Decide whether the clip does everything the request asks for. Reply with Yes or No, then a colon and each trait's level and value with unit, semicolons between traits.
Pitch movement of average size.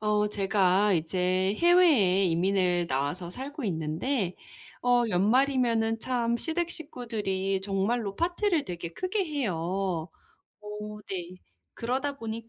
No: wide, 5.8 semitones